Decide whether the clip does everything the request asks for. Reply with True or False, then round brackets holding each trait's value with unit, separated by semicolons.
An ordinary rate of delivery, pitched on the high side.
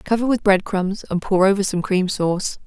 False (225 wpm; 195 Hz)